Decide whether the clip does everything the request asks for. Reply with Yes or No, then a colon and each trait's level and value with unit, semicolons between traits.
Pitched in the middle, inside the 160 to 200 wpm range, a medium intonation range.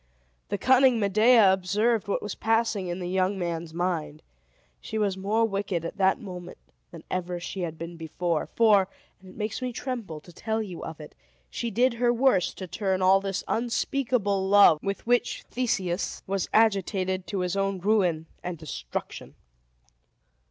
No: high, 195 Hz; average, 165 wpm; average, 3.6 semitones